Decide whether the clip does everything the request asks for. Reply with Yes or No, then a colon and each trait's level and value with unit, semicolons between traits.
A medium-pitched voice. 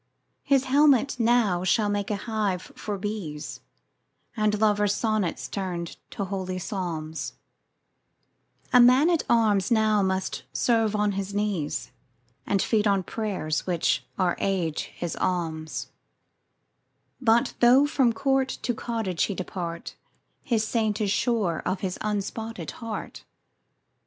No: high, 205 Hz